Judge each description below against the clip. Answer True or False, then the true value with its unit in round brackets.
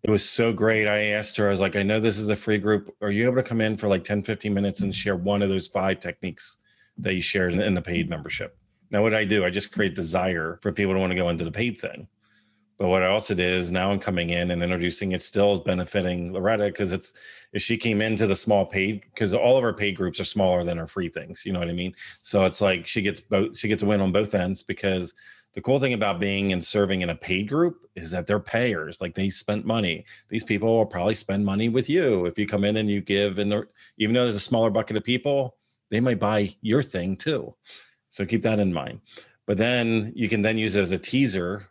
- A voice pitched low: True (100 Hz)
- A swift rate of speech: True (260 wpm)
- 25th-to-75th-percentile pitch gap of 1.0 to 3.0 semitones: True (2.5 semitones)